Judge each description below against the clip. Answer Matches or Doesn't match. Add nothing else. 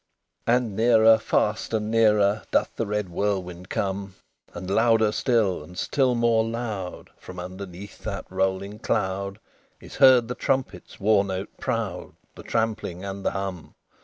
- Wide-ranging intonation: Doesn't match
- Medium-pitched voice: Doesn't match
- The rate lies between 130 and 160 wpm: Matches